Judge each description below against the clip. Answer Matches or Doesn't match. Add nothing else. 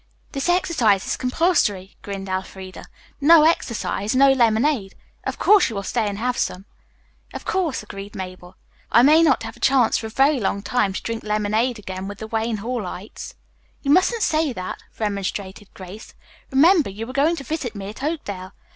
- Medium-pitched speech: Doesn't match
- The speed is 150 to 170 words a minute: Doesn't match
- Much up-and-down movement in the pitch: Matches